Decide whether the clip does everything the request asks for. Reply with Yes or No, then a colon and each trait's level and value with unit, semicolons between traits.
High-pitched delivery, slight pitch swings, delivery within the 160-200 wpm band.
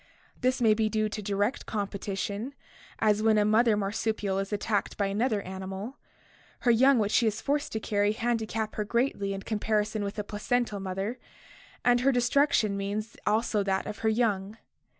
Yes: high, 215 Hz; narrow, 2.3 semitones; average, 170 wpm